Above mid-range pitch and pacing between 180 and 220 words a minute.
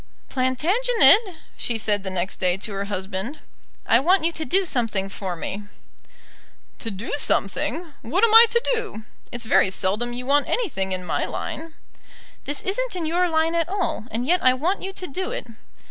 Yes: very high, 275 Hz; average, 185 wpm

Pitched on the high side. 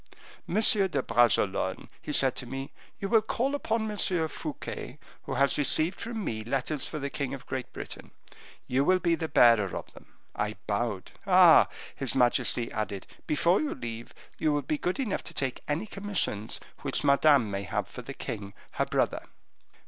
No: medium, 140 Hz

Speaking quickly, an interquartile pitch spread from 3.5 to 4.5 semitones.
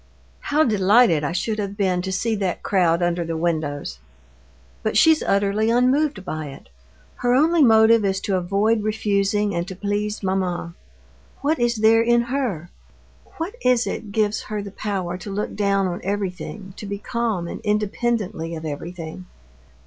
No: average, 160 wpm; average, 3.9 semitones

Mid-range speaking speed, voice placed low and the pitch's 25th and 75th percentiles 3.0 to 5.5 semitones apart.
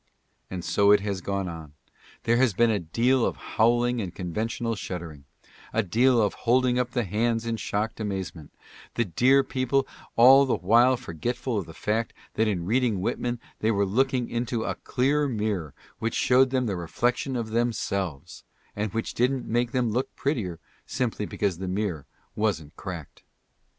Yes: average, 175 wpm; low, 110 Hz; average, 4.2 semitones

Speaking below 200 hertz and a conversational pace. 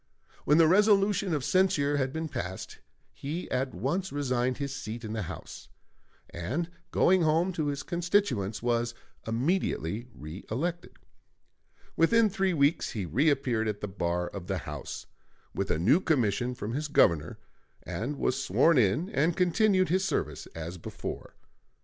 Yes: medium, 140 Hz; average, 150 wpm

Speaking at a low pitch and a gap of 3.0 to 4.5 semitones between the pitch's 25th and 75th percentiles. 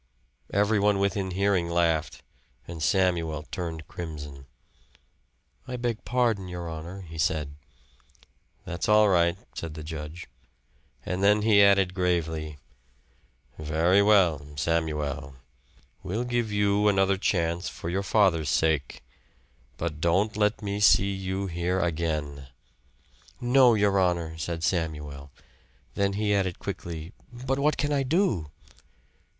Yes: very low, 90 Hz; average, 4.0 semitones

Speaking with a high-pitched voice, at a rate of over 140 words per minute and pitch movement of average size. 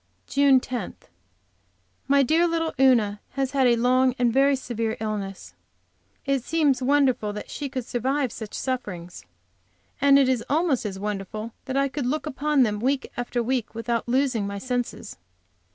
Yes: very high, 255 Hz; average, 160 wpm; average, 3.8 semitones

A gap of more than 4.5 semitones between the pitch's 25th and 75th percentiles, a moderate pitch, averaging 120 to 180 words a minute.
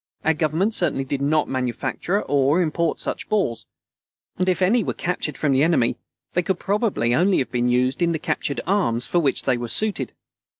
No: wide, 5.6 semitones; medium, 155 Hz; average, 195 wpm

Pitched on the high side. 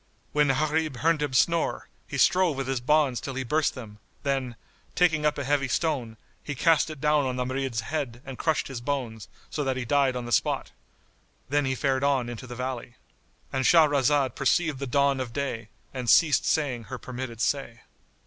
No: low, 135 Hz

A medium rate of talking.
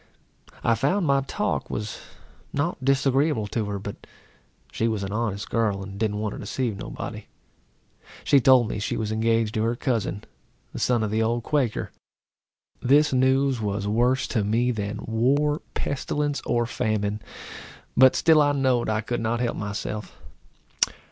Yes: average, 160 wpm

